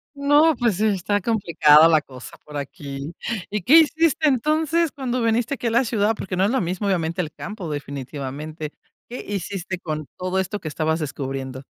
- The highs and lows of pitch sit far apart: Yes, wide, 7.6 semitones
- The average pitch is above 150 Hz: Yes, high, 190 Hz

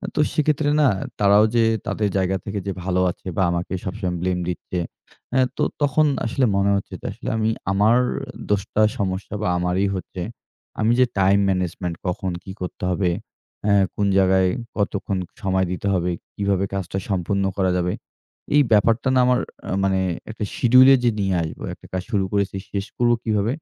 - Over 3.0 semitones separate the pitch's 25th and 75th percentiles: No, average, 2.7 semitones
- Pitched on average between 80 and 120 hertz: Yes, low, 100 Hz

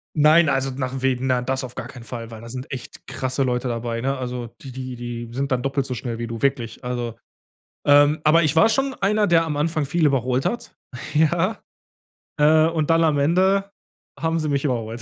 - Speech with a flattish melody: No, average, 4.1 semitones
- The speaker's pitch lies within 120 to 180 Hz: Yes, low, 135 Hz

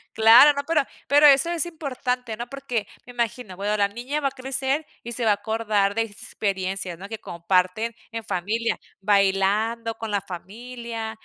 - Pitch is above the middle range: Yes, high, 225 Hz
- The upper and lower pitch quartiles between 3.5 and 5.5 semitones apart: Yes, average, 3.8 semitones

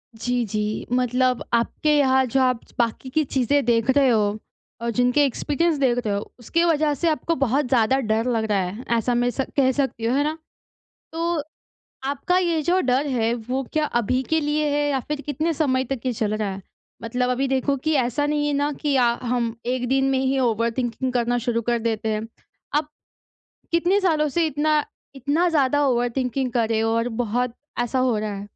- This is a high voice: Yes, very high, 260 Hz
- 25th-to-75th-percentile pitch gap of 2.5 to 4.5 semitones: Yes, average, 3.8 semitones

